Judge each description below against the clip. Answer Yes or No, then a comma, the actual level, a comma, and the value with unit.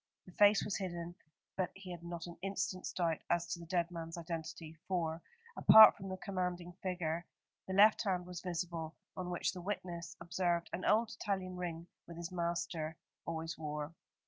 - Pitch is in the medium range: Yes, medium, 175 Hz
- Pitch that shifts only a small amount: Yes, narrow, 1.7 semitones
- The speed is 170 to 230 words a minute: Yes, average, 175 wpm